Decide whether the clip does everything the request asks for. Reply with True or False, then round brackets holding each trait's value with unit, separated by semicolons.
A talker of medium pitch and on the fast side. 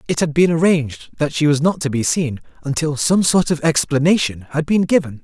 True (155 Hz; 220 wpm)